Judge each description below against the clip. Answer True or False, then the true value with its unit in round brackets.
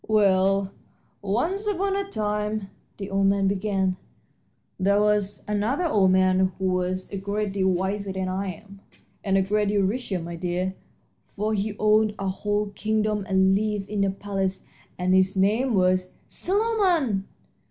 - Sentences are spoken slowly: False (160 wpm)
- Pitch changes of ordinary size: False (1.9 semitones)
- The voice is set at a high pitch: True (200 Hz)